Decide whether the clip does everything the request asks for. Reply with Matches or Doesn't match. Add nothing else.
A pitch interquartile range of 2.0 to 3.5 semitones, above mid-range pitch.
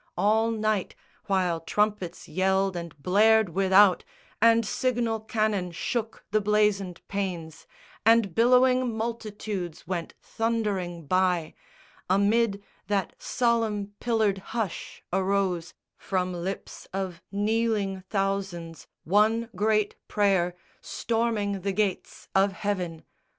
Matches